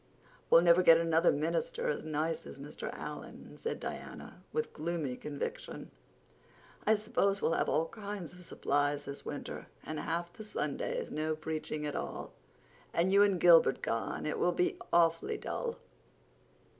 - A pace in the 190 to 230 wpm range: No, average, 150 wpm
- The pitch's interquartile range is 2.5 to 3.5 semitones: No, average, 4.7 semitones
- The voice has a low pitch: No, medium, 170 Hz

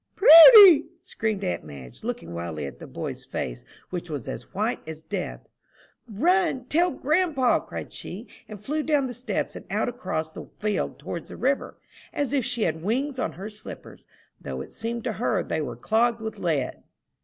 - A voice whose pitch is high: Yes, high, 220 Hz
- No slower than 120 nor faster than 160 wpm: No, average, 180 wpm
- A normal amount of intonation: No, wide, 9.0 semitones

